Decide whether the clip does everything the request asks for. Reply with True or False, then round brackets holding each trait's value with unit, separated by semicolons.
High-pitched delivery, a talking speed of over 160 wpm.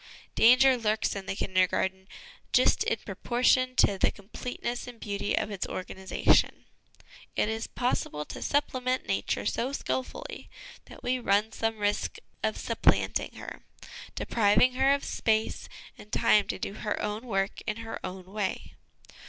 False (220 Hz; 150 wpm)